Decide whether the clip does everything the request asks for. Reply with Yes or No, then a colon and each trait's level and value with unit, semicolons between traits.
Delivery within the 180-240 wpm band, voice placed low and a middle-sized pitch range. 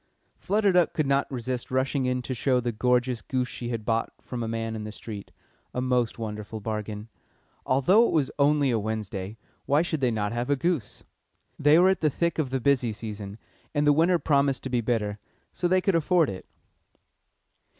Yes: average, 200 wpm; low, 125 Hz; average, 4.7 semitones